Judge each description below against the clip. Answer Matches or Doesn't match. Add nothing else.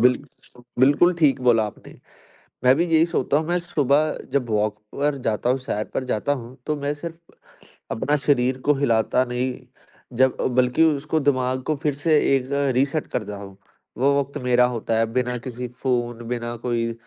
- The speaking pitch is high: Doesn't match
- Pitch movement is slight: Doesn't match